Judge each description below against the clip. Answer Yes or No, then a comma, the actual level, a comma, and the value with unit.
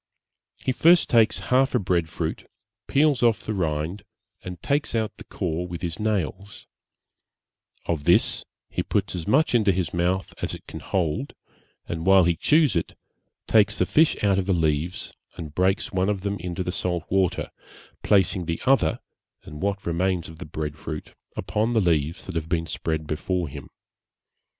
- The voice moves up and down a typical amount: Yes, average, 3.9 semitones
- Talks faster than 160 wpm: Yes, average, 175 wpm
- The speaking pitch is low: Yes, very low, 90 Hz